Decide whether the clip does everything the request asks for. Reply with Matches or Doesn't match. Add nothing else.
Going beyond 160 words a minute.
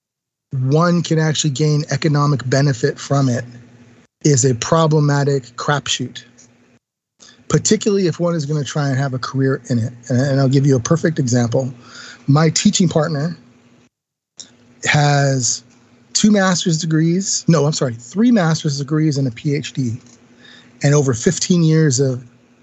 Doesn't match